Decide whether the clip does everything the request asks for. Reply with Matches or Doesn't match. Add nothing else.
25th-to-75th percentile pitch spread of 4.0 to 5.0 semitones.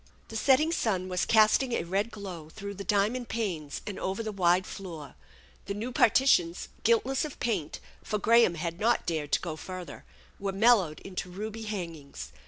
Matches